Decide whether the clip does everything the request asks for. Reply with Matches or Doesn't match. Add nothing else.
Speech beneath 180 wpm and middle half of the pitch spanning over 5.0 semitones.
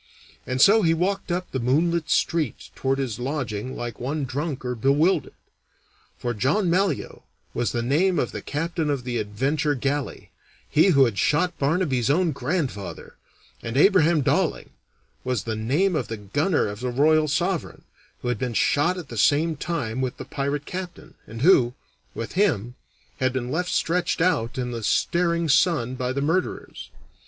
Matches